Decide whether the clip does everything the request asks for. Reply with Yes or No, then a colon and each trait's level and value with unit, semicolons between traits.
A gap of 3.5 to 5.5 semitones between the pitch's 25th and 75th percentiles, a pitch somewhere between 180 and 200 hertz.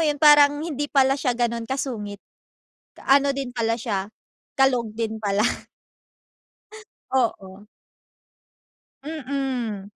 No: average, 4.0 semitones; very high, 250 Hz